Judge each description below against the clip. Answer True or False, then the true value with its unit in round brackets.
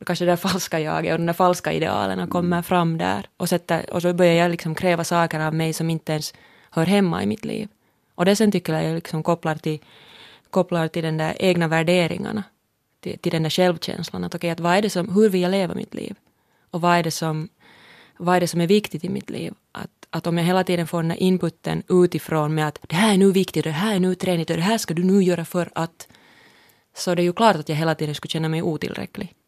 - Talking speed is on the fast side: True (245 wpm)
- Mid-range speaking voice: True (175 Hz)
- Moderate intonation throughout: False (2.3 semitones)